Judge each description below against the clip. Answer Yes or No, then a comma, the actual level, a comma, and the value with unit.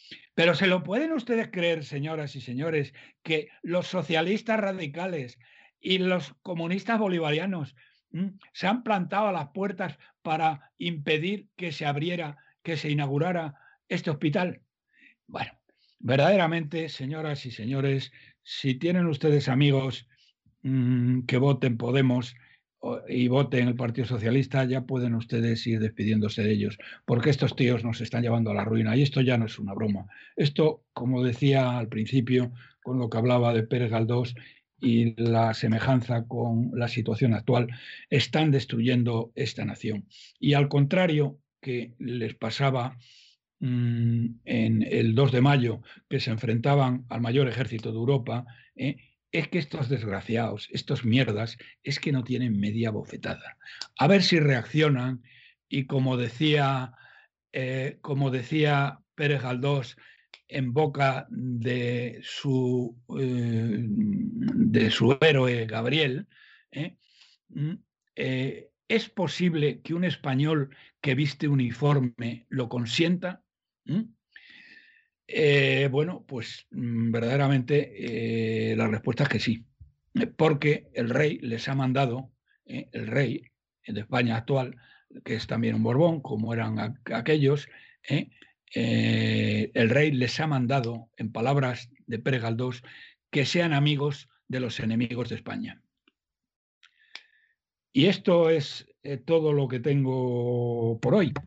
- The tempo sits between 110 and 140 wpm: Yes, average, 130 wpm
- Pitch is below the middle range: Yes, low, 130 Hz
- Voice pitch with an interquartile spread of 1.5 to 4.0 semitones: No, average, 4.4 semitones